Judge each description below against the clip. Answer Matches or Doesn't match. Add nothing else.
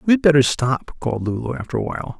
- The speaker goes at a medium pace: Doesn't match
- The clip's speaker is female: Doesn't match